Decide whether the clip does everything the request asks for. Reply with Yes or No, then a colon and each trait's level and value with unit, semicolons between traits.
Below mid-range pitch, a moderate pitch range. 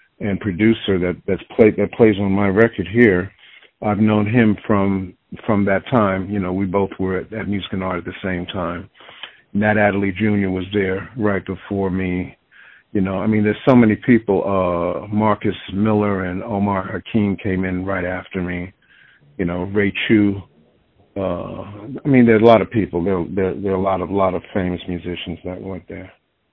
No: very low, 95 Hz; narrow, 2.3 semitones